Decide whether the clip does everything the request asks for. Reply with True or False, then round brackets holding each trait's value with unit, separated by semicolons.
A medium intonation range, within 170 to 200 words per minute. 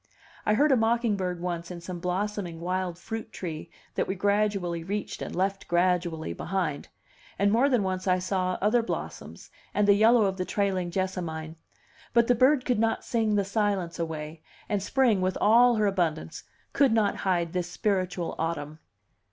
True (3.5 semitones; 175 wpm)